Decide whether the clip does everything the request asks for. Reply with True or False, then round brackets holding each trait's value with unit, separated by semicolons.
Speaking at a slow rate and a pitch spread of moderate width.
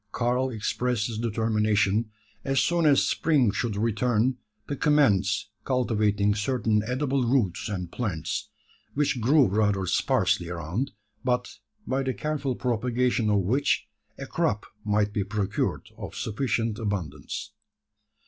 True (125 wpm; 3.7 semitones)